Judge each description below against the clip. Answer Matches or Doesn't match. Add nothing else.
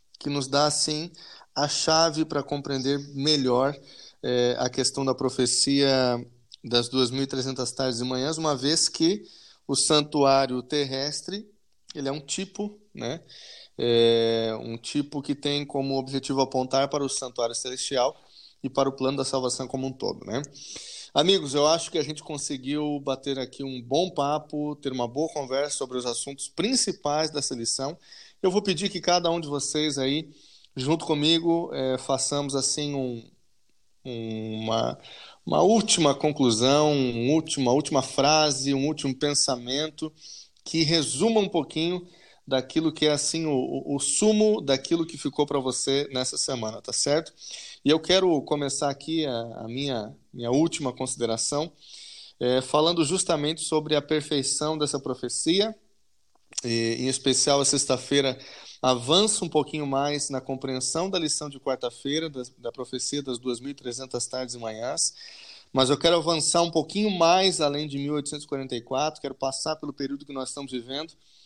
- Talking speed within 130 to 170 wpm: Matches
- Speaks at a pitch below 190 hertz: Matches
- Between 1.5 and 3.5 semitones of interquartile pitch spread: Matches